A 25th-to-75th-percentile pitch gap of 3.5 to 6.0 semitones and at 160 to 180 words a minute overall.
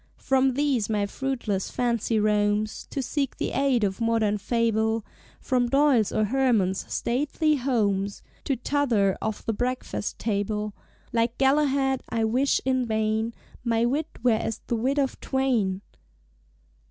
No: average, 3.8 semitones; average, 140 wpm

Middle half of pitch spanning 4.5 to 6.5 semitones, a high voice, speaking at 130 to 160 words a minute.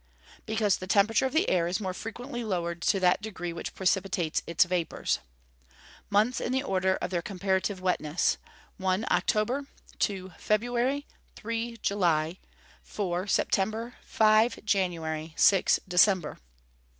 No: average, 3.5 semitones; high, 195 Hz; slow, 135 wpm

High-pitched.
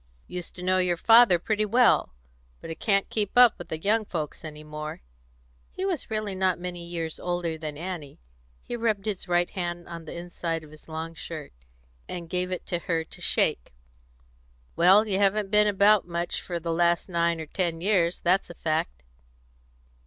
No: medium, 175 Hz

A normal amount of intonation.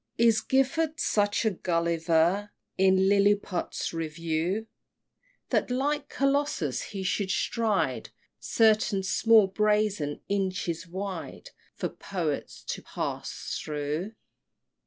Yes: average, 4.6 semitones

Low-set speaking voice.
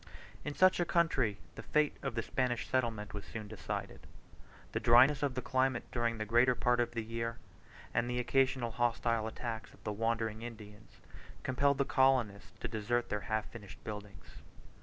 Yes: low, 115 Hz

